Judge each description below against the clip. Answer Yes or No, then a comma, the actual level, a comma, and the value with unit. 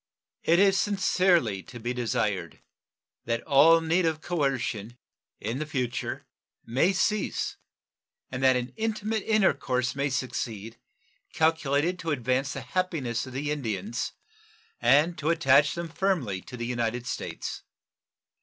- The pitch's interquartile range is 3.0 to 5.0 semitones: No, wide, 5.6 semitones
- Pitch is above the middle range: No, medium, 140 Hz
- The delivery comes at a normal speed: No, slow, 125 wpm